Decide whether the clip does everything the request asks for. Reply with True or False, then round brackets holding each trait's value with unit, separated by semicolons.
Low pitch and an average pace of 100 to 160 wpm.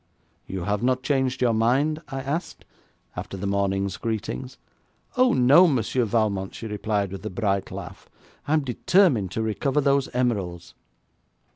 True (115 Hz; 150 wpm)